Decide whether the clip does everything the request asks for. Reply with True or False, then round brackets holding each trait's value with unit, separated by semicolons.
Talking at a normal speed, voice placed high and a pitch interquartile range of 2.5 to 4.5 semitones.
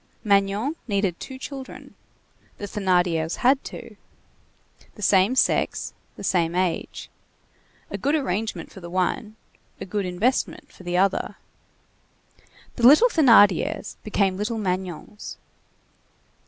False (115 wpm; 200 Hz; 4.2 semitones)